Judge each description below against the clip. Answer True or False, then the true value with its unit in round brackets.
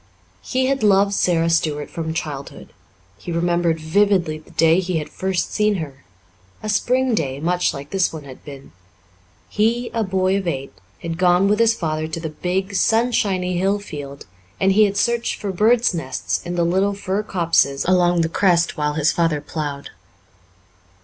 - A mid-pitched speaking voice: True (175 Hz)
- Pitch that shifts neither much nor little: True (4.3 semitones)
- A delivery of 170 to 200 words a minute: True (175 wpm)